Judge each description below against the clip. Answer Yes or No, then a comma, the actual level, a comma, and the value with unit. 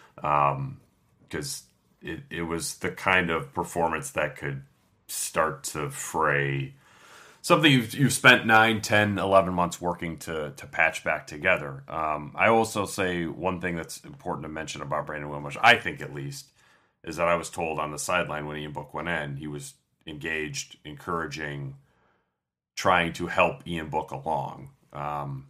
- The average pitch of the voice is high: No, very low, 75 Hz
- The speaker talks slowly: No, average, 160 wpm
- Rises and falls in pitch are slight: No, average, 3.6 semitones